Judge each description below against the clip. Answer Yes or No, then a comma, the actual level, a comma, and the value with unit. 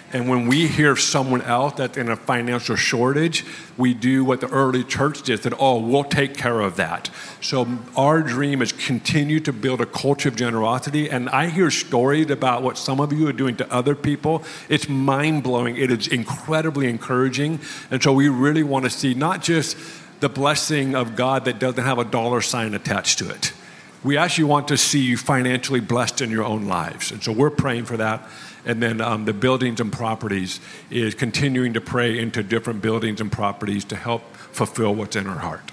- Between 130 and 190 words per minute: No, average, 200 wpm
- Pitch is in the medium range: No, low, 130 Hz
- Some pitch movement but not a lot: Yes, average, 3.3 semitones